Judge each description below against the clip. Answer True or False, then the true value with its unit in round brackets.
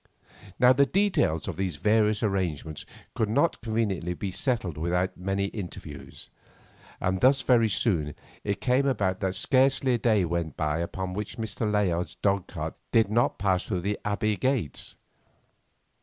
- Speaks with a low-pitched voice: True (100 Hz)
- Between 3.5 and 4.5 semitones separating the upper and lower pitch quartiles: True (4.2 semitones)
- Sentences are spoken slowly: False (155 wpm)